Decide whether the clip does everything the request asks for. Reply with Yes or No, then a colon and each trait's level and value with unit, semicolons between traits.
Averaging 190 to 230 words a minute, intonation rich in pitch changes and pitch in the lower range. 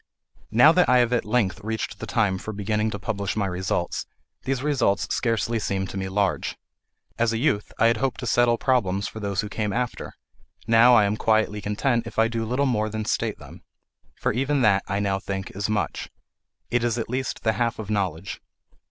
No: fast, 205 wpm; average, 3.1 semitones; low, 110 Hz